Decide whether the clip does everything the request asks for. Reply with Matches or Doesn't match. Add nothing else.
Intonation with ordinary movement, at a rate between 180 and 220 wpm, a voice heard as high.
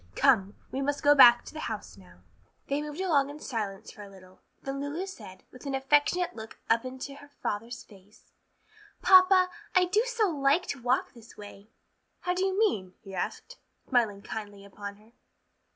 Doesn't match